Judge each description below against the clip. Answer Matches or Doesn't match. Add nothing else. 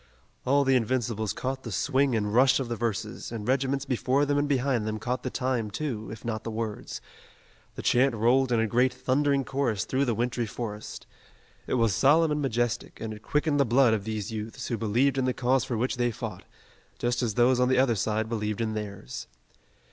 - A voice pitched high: Doesn't match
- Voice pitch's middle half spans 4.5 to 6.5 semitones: Doesn't match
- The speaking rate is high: Matches